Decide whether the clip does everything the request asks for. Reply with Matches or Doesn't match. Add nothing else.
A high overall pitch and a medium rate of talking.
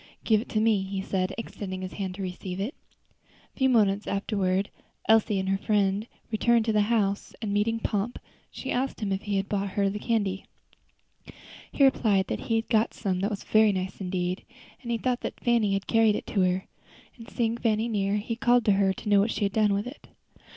Doesn't match